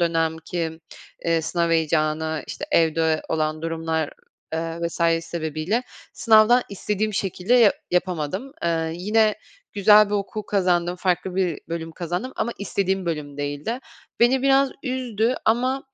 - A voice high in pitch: No, medium, 175 Hz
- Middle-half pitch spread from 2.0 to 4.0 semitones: No, average, 4.7 semitones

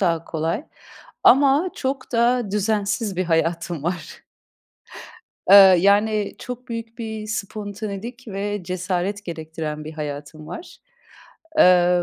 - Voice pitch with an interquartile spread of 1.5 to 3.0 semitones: No, average, 4.5 semitones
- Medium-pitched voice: No, high, 200 Hz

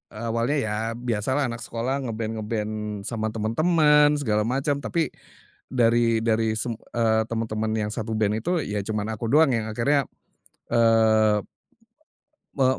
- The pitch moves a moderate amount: Yes, average, 3.3 semitones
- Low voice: Yes, low, 115 Hz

